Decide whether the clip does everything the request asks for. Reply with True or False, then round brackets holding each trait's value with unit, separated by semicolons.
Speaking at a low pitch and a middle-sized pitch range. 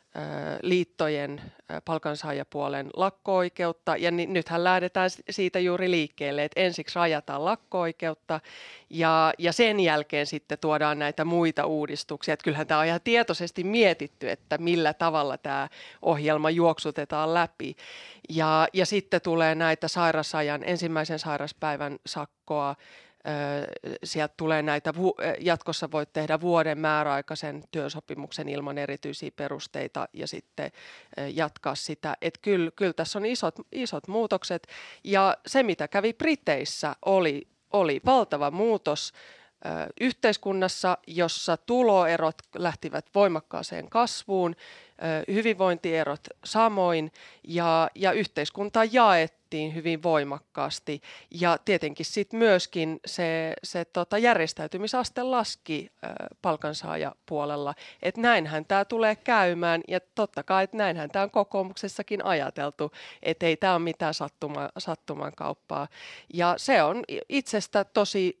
False (165 Hz; 3.8 semitones)